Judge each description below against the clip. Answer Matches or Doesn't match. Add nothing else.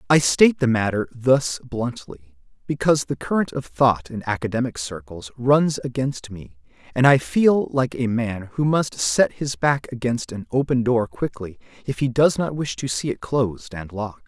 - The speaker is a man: Matches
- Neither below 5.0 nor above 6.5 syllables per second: Doesn't match